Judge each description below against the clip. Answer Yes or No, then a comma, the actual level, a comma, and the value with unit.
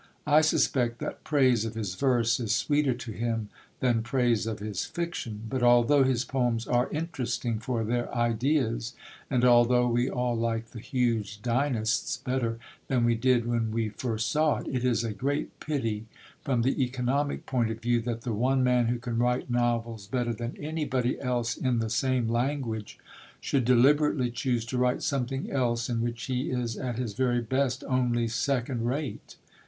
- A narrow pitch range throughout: Yes, narrow, 2.1 semitones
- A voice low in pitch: Yes, low, 120 Hz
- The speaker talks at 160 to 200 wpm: Yes, average, 175 wpm